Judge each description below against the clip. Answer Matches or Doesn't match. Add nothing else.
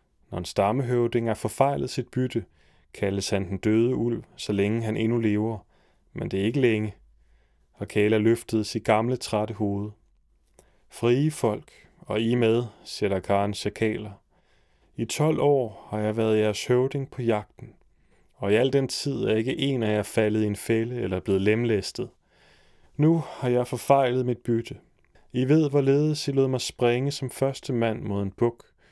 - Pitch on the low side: Matches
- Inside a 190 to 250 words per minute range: Doesn't match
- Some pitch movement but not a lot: Matches